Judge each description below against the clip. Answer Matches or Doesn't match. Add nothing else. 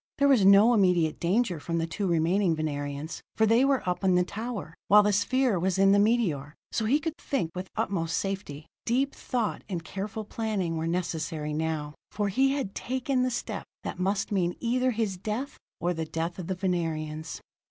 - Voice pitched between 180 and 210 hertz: Matches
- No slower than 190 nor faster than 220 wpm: Matches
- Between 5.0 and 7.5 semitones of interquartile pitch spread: Matches